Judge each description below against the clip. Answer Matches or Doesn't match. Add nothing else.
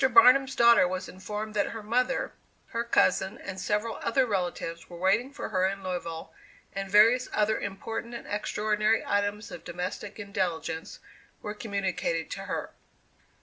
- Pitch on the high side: Matches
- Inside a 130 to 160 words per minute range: Matches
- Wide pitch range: Doesn't match